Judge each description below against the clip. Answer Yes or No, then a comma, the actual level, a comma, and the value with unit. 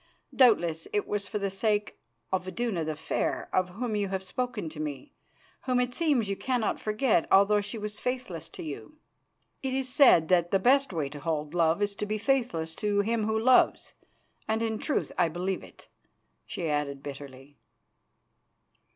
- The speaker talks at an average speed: Yes, average, 175 wpm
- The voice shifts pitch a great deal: Yes, wide, 6.0 semitones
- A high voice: Yes, high, 205 Hz